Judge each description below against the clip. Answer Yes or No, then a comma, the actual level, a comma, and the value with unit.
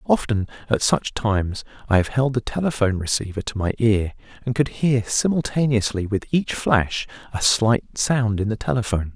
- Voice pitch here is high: No, low, 115 Hz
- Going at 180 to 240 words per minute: No, average, 170 wpm